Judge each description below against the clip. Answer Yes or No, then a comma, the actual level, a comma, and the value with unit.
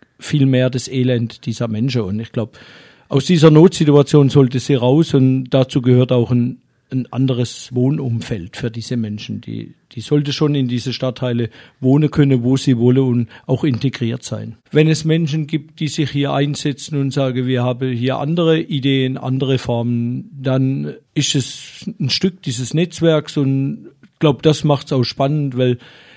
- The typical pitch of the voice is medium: No, low, 130 Hz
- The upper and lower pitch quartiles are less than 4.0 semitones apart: Yes, average, 3.0 semitones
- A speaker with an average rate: Yes, average, 170 wpm